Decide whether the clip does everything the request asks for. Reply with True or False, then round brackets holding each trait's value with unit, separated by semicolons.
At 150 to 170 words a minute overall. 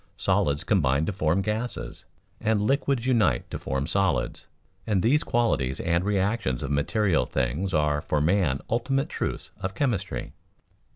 False (140 wpm)